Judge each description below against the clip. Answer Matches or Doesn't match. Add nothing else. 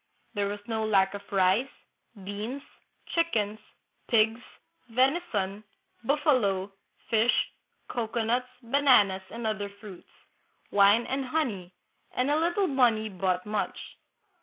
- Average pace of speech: Doesn't match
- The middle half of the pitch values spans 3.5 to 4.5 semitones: Matches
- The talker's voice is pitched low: Doesn't match